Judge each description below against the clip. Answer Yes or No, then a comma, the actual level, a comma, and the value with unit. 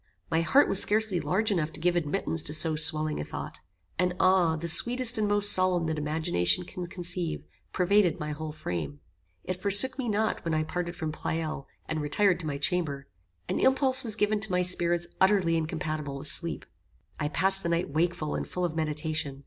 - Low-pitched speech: No, medium, 170 Hz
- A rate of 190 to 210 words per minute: Yes, average, 195 wpm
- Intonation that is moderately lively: Yes, average, 3.6 semitones